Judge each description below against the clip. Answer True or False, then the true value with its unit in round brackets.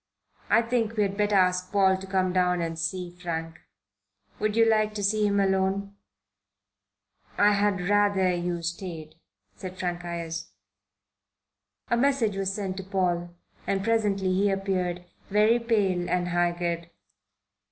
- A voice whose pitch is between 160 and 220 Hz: True (190 Hz)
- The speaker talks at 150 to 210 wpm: False (140 wpm)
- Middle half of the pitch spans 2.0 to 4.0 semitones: True (2.6 semitones)